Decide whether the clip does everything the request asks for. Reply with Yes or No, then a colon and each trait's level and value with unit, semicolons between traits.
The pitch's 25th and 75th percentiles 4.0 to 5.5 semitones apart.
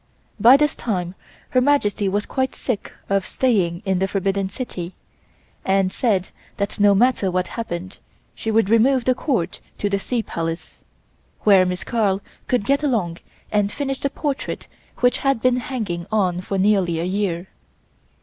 Yes: average, 4.9 semitones